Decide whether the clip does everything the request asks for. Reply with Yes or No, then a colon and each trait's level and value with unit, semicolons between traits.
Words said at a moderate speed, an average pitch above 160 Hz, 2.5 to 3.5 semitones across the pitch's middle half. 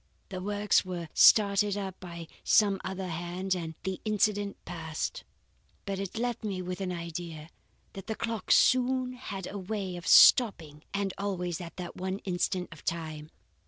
Yes: average, 160 wpm; high, 190 Hz; average, 2.8 semitones